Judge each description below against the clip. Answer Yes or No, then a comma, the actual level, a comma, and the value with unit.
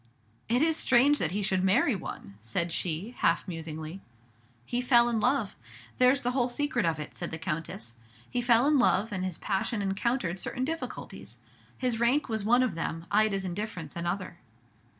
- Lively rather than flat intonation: Yes, wide, 6.2 semitones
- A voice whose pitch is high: Yes, high, 205 Hz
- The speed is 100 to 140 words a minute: No, average, 175 wpm